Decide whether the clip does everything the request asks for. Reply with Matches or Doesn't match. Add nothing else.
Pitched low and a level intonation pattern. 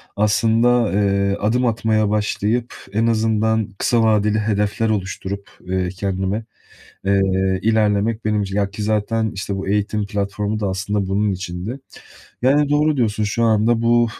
Matches